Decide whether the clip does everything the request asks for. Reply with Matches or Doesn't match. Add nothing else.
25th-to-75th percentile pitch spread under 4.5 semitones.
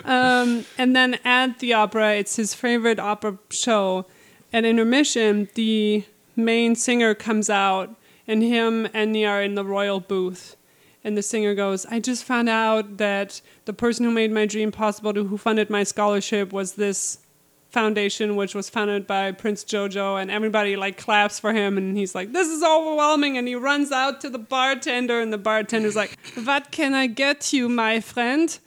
Matches